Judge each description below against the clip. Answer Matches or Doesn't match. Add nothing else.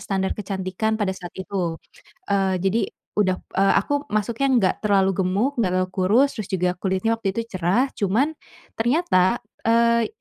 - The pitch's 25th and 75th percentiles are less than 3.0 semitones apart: Doesn't match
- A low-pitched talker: Doesn't match